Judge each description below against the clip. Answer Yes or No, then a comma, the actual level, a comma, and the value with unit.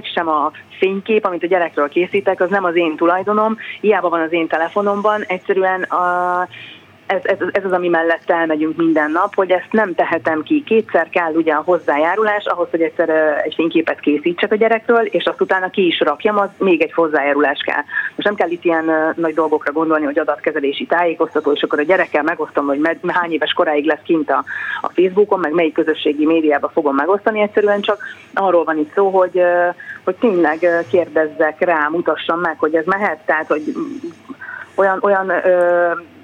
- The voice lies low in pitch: No, medium, 175 Hz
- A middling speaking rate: No, fast, 175 wpm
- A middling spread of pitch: Yes, average, 3.7 semitones